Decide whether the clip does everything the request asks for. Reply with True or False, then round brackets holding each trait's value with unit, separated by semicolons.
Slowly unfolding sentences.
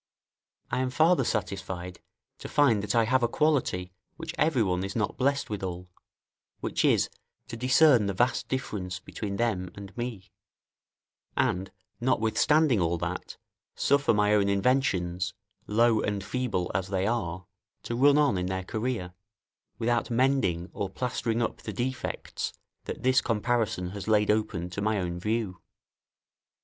False (150 wpm)